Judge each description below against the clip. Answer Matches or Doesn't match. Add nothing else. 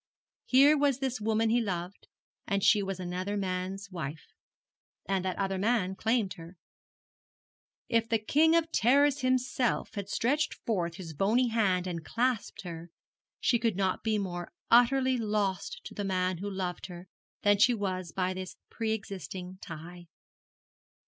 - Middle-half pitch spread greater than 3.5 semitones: Matches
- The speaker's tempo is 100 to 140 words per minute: Doesn't match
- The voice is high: Matches